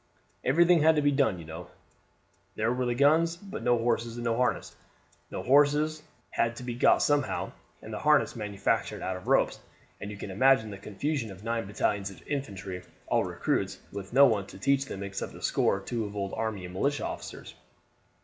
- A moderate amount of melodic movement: No, wide, 5.9 semitones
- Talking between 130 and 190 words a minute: No, average, 200 wpm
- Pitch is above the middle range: No, low, 115 Hz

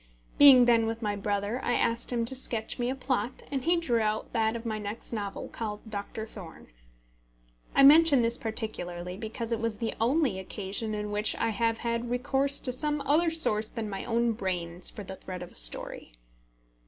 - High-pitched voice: Yes, high, 225 Hz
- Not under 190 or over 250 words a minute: Yes, average, 195 wpm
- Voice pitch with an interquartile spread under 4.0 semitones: Yes, average, 3.0 semitones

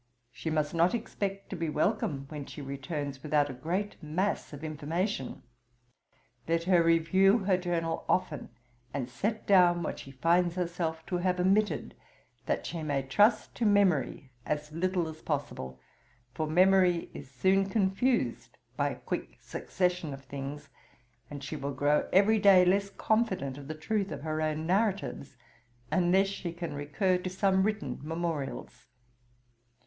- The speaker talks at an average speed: Yes, average, 155 wpm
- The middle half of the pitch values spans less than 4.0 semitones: No, average, 4.6 semitones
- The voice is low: No, medium, 170 Hz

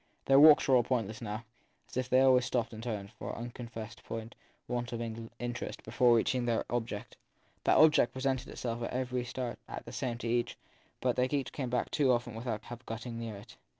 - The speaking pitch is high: No, low, 120 Hz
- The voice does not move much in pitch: Yes, narrow, 1.8 semitones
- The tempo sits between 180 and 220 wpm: Yes, fast, 205 wpm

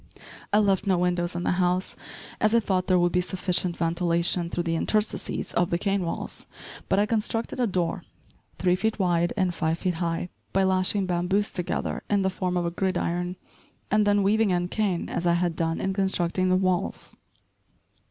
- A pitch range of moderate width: No, narrow, 2.0 semitones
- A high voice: No, medium, 180 Hz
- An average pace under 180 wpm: No, average, 190 wpm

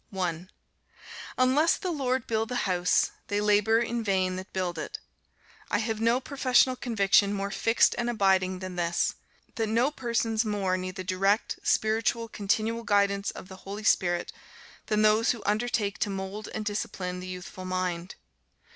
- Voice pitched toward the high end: Yes, high, 205 Hz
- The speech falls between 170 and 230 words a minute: No, average, 160 wpm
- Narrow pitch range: No, average, 3.5 semitones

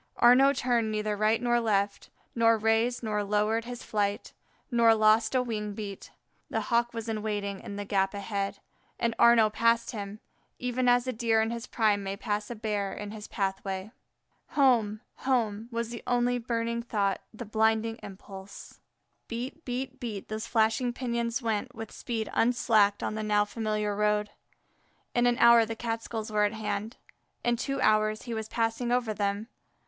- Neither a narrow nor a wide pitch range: No, narrow, 2.1 semitones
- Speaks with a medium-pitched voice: No, high, 220 Hz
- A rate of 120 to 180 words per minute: Yes, average, 175 wpm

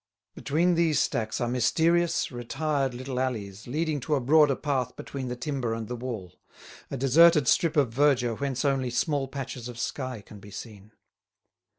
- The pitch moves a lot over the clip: No, average, 3.6 semitones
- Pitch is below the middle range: Yes, low, 130 Hz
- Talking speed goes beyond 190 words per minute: No, average, 170 wpm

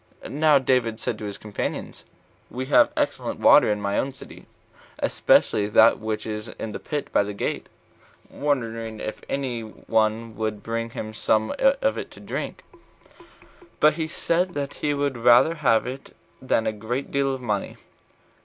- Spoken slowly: No, average, 165 wpm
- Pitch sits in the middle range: No, low, 115 Hz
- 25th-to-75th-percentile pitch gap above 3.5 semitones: Yes, average, 4.3 semitones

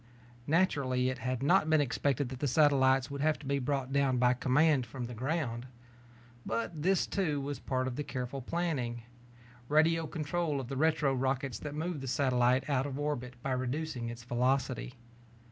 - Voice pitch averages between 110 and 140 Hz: Yes, low, 135 Hz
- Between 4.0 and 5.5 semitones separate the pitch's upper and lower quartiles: No, average, 2.8 semitones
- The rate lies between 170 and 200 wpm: Yes, average, 180 wpm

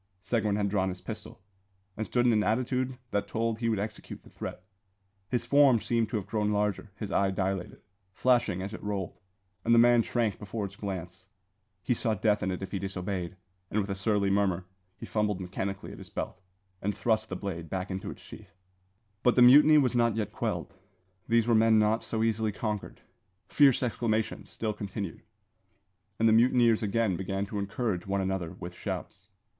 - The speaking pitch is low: Yes, low, 105 Hz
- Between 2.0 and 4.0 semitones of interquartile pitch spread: Yes, average, 3.0 semitones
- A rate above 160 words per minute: Yes, average, 190 wpm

